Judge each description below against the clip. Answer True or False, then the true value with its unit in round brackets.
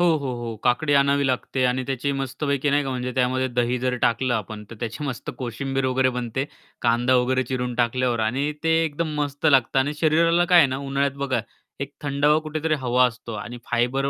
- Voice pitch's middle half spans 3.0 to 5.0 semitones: False (2.4 semitones)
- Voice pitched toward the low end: True (130 Hz)